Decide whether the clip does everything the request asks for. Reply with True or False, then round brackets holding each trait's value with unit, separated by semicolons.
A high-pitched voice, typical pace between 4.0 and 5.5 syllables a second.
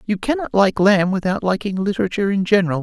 False (195 Hz; 6.5 syllables/s)